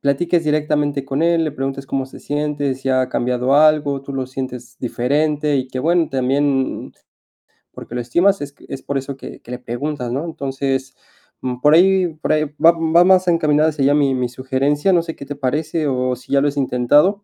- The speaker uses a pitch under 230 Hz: Yes, medium, 140 Hz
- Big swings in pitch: No, average, 2.8 semitones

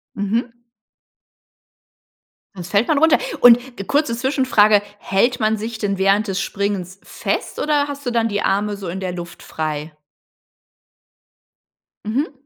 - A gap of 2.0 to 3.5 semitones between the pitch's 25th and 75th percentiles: No, average, 4.1 semitones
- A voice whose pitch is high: Yes, high, 210 Hz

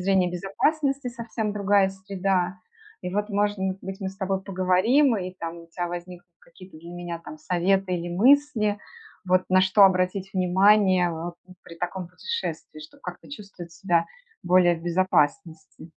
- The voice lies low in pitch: No, medium, 185 Hz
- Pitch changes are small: Yes, narrow, 2.3 semitones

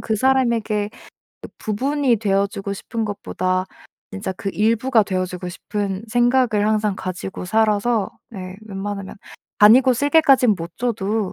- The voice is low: No, high, 210 Hz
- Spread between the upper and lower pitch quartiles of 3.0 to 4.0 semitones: Yes, average, 3.4 semitones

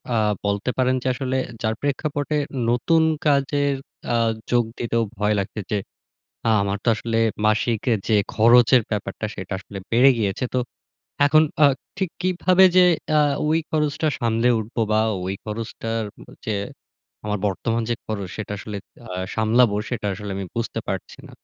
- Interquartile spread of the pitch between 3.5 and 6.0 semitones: Yes, average, 4.2 semitones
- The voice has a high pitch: No, low, 115 Hz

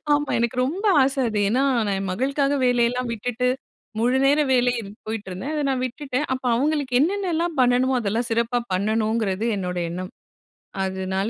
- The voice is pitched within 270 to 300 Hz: No, high, 245 Hz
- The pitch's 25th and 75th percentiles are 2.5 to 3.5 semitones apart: No, average, 4.1 semitones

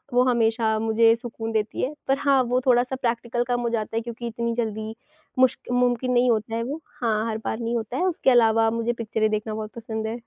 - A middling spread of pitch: No, narrow, 1.7 semitones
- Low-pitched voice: No, high, 230 Hz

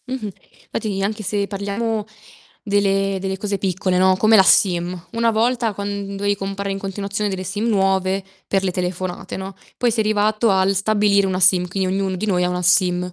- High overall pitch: Yes, high, 195 Hz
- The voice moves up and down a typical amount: No, narrow, 1.7 semitones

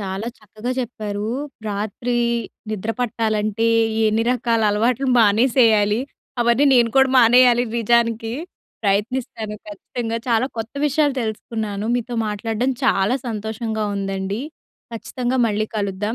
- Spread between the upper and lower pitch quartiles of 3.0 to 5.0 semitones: No, narrow, 2.4 semitones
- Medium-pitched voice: No, high, 225 Hz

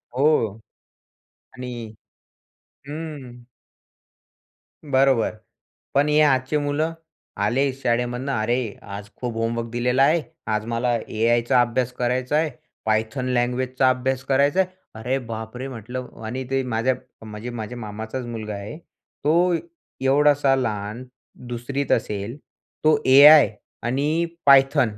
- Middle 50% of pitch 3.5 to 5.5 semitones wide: No, average, 2.8 semitones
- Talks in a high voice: No, low, 125 Hz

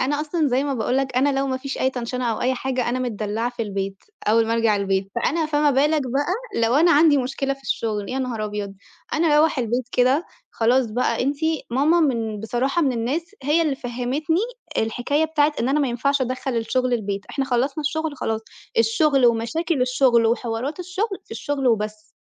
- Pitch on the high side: Yes, very high, 255 Hz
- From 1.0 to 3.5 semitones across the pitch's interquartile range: No, average, 4.1 semitones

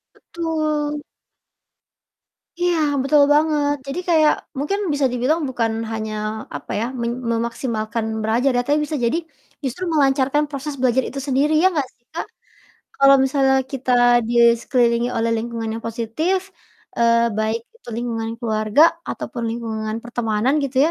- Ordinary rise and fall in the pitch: Yes, average, 4.2 semitones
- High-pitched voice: Yes, very high, 255 Hz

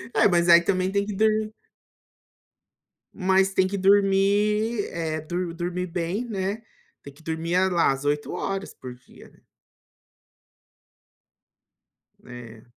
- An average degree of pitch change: Yes, average, 3.5 semitones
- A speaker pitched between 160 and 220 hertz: Yes, medium, 185 Hz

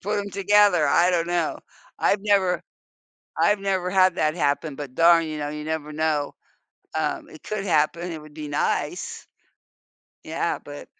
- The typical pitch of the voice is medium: Yes, medium, 170 Hz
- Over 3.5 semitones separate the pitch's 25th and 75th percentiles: Yes, average, 4.3 semitones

